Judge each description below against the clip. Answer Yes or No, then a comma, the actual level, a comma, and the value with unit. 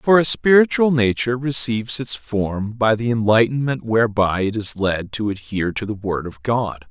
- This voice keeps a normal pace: Yes, average, 180 wpm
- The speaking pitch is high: No, low, 115 Hz